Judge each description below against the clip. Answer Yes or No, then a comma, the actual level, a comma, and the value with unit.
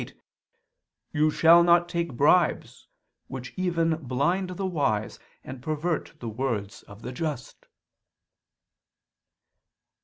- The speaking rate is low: Yes, slow, 100 wpm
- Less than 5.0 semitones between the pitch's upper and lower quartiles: No, average, 5.3 semitones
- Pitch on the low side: No, medium, 155 Hz